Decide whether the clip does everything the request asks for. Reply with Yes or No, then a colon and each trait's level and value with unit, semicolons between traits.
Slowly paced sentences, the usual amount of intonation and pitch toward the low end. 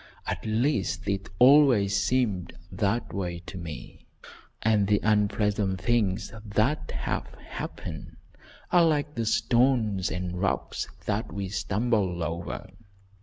Yes: slow, 120 wpm; average, 3.7 semitones; low, 105 Hz